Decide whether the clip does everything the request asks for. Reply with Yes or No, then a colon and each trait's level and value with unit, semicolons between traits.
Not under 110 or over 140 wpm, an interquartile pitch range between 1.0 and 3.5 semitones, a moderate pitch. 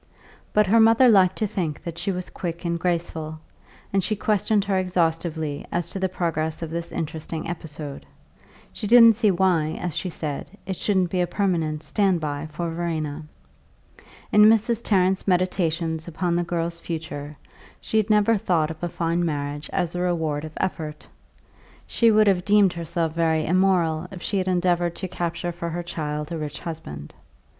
No: average, 175 wpm; average, 3.0 semitones; medium, 170 Hz